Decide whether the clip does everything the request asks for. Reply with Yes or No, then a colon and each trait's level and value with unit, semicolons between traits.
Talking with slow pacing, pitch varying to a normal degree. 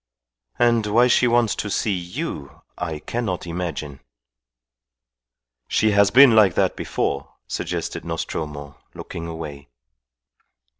No: slow, 110 wpm; wide, 6.8 semitones